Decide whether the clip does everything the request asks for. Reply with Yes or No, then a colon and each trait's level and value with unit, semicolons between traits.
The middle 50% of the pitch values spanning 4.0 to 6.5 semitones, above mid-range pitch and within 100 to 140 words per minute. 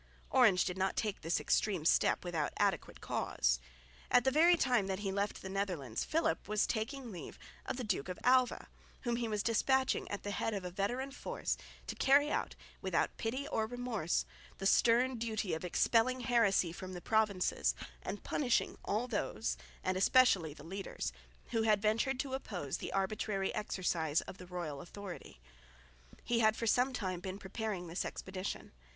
No: average, 4.8 semitones; high, 205 Hz; average, 175 wpm